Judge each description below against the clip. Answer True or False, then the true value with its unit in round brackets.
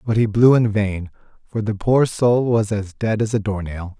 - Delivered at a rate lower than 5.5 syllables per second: True (4.5 syllables/s)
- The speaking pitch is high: False (110 Hz)